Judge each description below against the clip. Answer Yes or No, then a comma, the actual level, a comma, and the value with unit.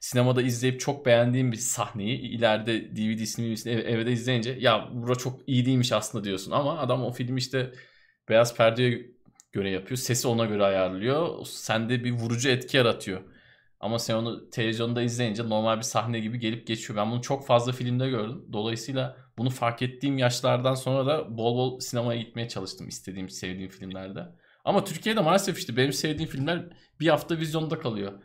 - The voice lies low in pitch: Yes, low, 120 Hz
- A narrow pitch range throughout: Yes, narrow, 2.3 semitones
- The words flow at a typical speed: No, fast, 170 wpm